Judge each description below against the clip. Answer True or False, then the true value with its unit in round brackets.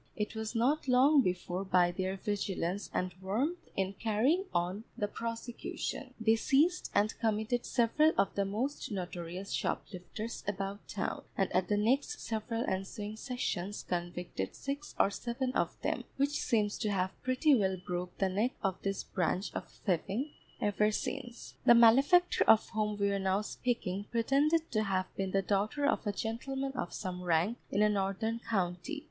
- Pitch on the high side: True (210 Hz)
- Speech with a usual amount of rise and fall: True (4.2 semitones)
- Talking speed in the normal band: True (165 wpm)